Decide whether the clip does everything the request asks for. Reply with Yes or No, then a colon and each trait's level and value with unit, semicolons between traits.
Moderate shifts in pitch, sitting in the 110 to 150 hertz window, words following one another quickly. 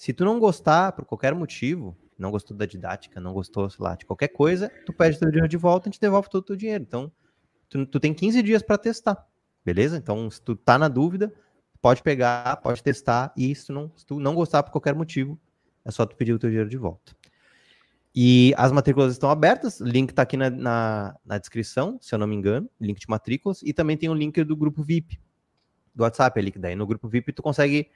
No: wide, 6.0 semitones; medium, 140 Hz; fast, 240 wpm